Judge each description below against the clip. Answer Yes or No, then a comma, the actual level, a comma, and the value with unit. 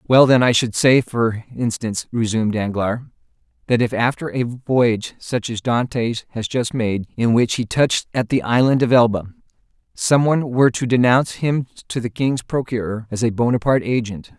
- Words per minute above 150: Yes, average, 180 wpm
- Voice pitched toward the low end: Yes, low, 120 Hz